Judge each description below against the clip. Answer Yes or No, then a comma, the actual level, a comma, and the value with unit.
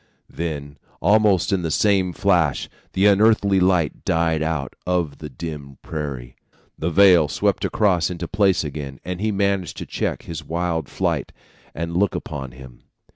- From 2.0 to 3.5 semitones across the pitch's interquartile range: No, average, 4.3 semitones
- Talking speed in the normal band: Yes, average, 155 wpm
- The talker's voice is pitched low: Yes, very low, 85 Hz